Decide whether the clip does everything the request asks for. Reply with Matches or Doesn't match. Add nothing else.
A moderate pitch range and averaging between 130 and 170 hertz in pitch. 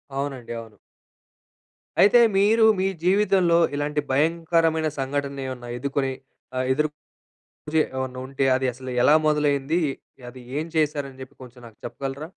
Matches